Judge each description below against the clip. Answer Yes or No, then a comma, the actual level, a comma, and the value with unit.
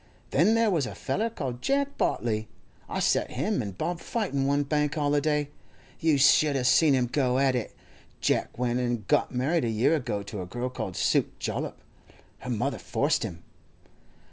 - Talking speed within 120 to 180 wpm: Yes, average, 175 wpm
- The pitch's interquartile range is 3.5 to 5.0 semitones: Yes, average, 3.9 semitones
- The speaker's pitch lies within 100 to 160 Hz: Yes, low, 135 Hz